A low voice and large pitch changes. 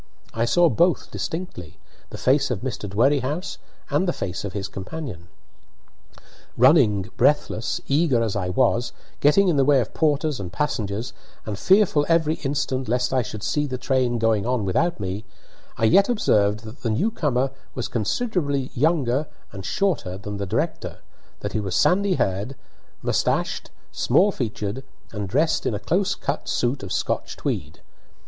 Yes: low, 125 Hz; wide, 6.5 semitones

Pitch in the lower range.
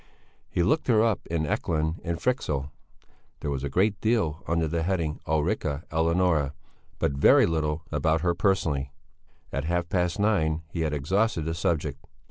Yes: very low, 80 Hz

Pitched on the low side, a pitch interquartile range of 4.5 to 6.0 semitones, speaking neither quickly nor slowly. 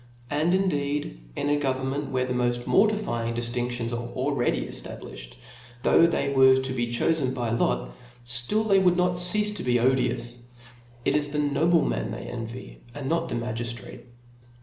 Yes: low, 130 Hz; average, 5.1 semitones; average, 165 wpm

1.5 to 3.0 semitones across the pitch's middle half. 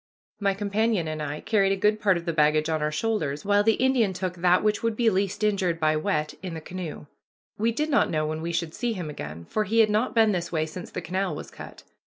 No: average, 5.2 semitones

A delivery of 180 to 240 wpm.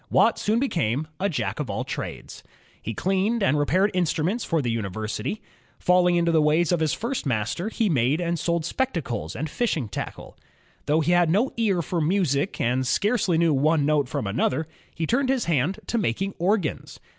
Yes: average, 185 wpm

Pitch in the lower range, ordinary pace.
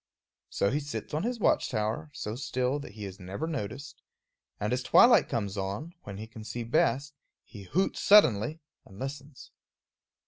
Yes: low, 125 Hz; average, 170 wpm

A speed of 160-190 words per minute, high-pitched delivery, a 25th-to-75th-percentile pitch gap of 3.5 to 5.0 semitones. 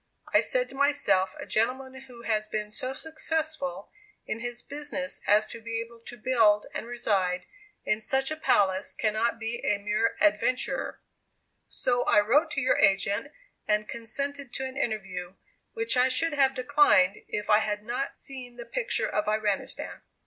Yes: average, 165 wpm; high, 240 Hz; average, 4.3 semitones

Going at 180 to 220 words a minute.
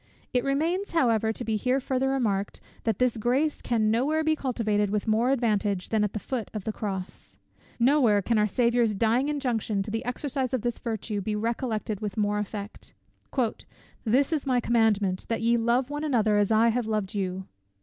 Yes: average, 195 wpm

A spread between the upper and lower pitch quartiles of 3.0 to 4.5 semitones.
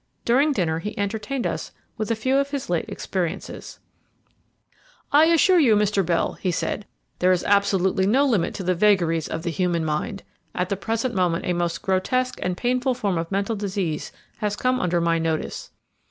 No: average, 5.0 semitones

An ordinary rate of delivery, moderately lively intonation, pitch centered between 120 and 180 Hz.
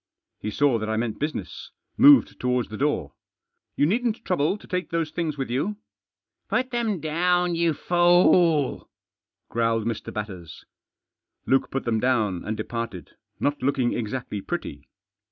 No: average, 150 wpm; wide, 7.4 semitones; low, 135 Hz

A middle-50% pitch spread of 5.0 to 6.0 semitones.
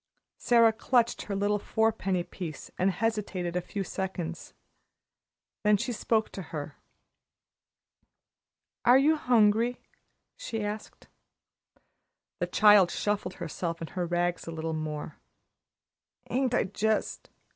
No: average, 4.2 semitones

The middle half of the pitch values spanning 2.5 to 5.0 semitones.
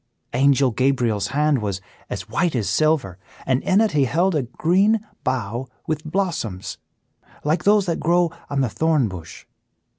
No: wide, 5.6 semitones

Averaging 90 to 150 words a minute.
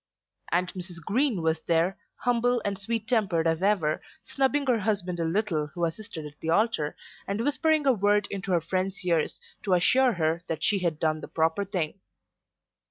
No: average, 180 wpm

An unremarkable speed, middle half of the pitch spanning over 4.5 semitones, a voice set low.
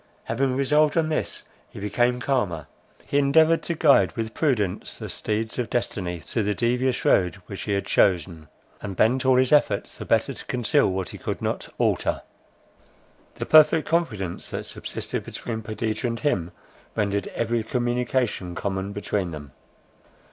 Yes: average, 160 wpm; average, 4.9 semitones; low, 115 Hz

